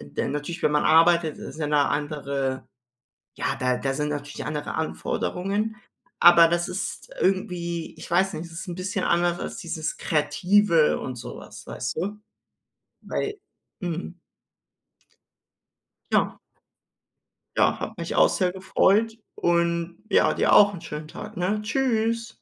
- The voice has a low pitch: No, medium, 170 Hz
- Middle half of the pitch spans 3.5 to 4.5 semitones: Yes, average, 4.2 semitones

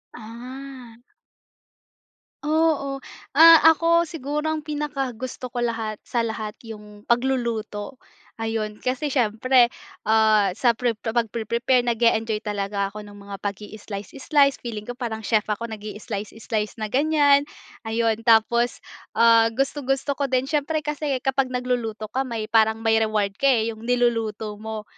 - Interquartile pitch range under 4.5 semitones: Yes, average, 3.5 semitones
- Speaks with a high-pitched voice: Yes, high, 235 Hz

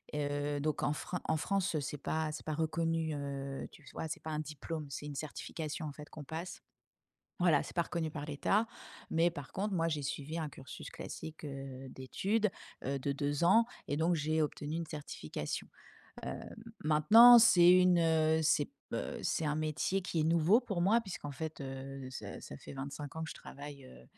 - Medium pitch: Yes, medium, 155 Hz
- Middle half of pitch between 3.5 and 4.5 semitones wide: No, average, 2.7 semitones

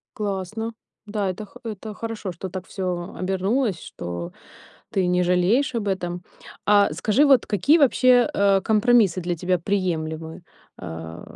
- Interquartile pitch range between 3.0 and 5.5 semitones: Yes, average, 3.4 semitones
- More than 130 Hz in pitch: Yes, high, 190 Hz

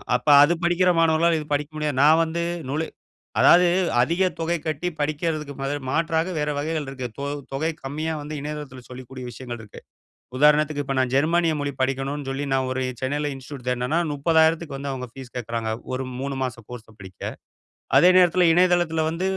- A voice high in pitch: No, medium, 145 Hz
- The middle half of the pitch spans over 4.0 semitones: No, average, 3.5 semitones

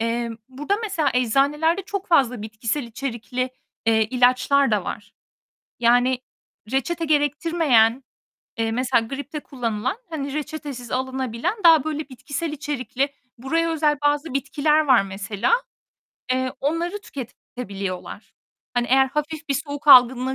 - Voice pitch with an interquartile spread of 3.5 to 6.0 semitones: Yes, average, 3.9 semitones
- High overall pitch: Yes, very high, 265 Hz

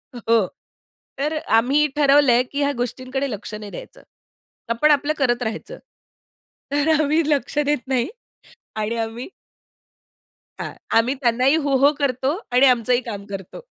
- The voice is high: Yes, very high, 255 Hz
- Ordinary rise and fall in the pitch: Yes, average, 3.7 semitones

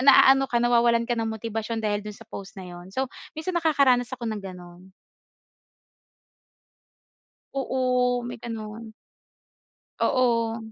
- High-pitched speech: Yes, high, 230 Hz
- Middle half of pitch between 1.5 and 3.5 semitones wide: Yes, average, 2.8 semitones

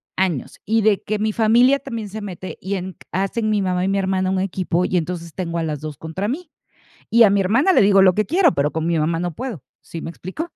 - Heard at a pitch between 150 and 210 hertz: Yes, high, 190 Hz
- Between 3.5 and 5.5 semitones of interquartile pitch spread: Yes, average, 4.0 semitones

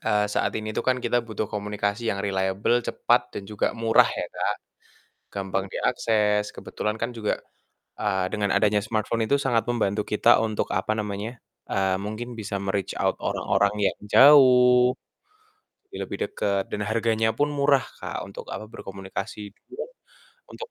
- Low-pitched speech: Yes, low, 105 Hz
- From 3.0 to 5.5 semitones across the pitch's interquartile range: No, narrow, 2.6 semitones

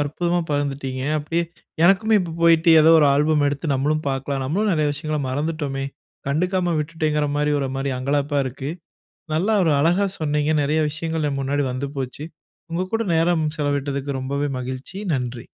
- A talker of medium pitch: Yes, medium, 150 Hz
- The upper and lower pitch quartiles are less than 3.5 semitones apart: Yes, average, 2.8 semitones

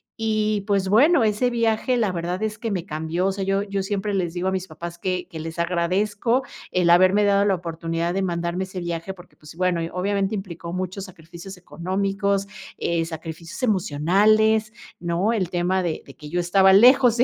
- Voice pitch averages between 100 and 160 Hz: No, high, 190 Hz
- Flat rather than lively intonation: No, average, 3.0 semitones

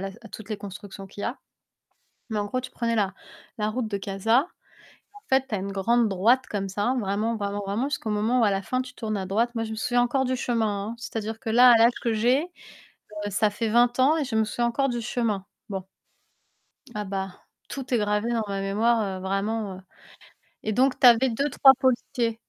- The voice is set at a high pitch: Yes, high, 225 Hz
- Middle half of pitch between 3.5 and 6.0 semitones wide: No, average, 3.1 semitones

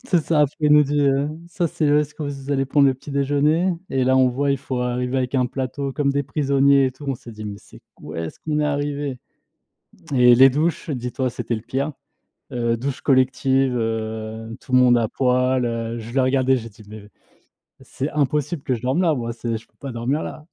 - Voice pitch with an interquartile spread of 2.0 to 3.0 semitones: Yes, average, 2.7 semitones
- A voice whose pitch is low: Yes, low, 130 Hz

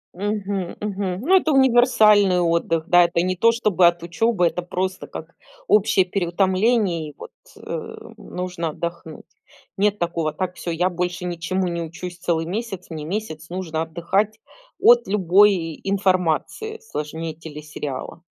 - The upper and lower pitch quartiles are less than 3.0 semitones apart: No, average, 3.3 semitones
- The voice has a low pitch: No, medium, 180 Hz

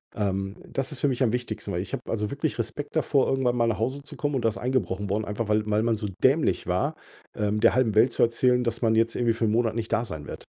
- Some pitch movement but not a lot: Yes, average, 3.3 semitones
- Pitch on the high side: No, low, 115 Hz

